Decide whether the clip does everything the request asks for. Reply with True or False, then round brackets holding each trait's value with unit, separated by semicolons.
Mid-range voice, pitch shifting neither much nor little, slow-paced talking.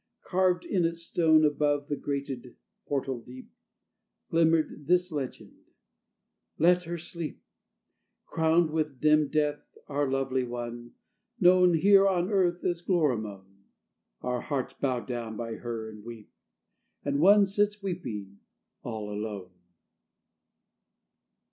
False (145 Hz; 6.2 semitones; 115 wpm)